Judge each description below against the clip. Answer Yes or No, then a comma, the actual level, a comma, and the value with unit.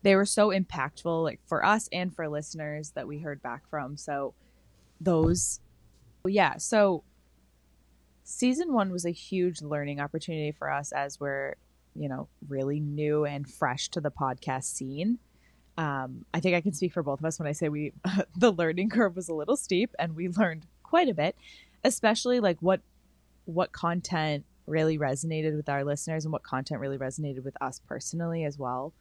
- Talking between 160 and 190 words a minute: Yes, average, 180 wpm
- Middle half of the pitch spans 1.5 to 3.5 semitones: No, average, 4.5 semitones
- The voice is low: No, medium, 155 Hz